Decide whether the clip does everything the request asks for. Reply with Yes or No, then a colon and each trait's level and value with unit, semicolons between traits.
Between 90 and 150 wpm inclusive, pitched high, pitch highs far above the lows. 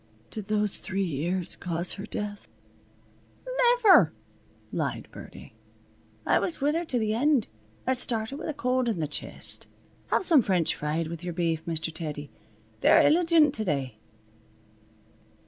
Yes: average, 145 wpm; high, 210 Hz; wide, 8.7 semitones